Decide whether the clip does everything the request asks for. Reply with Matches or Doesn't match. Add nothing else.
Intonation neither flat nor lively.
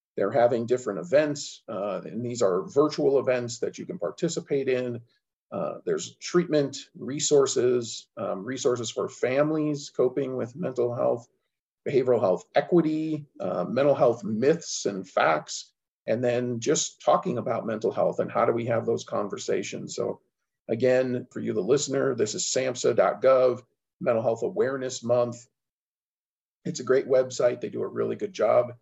Matches